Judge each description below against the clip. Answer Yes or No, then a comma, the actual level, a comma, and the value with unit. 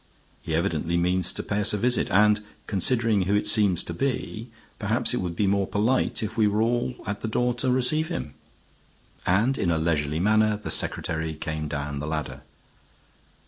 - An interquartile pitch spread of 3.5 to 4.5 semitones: No, average, 5.2 semitones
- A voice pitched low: Yes, low, 100 Hz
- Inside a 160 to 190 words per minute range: Yes, average, 185 wpm